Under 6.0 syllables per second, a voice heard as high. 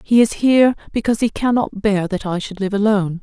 No: 6.1 syllables/s; high, 210 Hz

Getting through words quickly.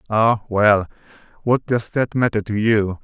No: average, 160 wpm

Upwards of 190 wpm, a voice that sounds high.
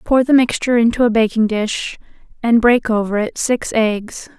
No: average, 180 wpm; high, 230 Hz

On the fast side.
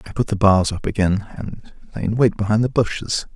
Yes: fast, 230 wpm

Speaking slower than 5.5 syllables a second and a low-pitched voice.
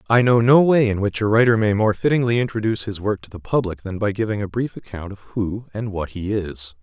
No: 6.0 syllables/s; low, 105 Hz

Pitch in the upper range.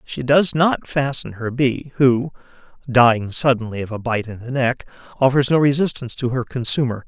No: low, 125 Hz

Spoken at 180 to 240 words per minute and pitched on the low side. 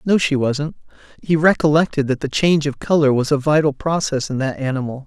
No: average, 200 wpm; medium, 145 Hz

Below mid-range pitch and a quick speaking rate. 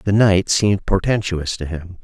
No: very low, 95 Hz; average, 175 wpm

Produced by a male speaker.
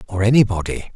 Yes: male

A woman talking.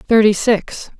Yes: female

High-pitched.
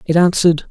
No: medium, 170 Hz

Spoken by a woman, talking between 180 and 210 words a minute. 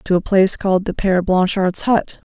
Yes: female; fast, 205 wpm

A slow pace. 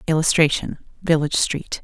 Yes: slow, 100 wpm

